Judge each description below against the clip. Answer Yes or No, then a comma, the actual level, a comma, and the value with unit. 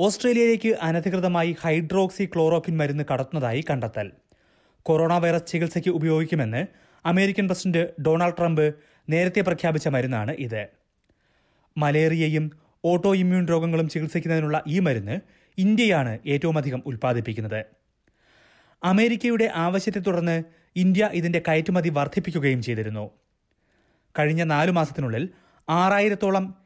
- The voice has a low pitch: No, medium, 165 Hz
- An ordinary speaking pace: Yes, average, 95 wpm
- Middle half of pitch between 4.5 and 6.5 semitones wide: No, average, 3.8 semitones